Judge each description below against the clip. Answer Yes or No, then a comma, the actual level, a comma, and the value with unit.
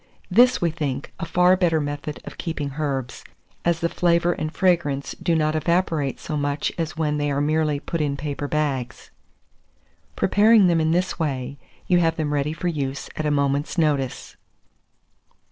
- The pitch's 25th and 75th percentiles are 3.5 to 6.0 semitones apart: No, average, 3.0 semitones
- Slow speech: No, average, 170 wpm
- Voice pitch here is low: No, medium, 155 Hz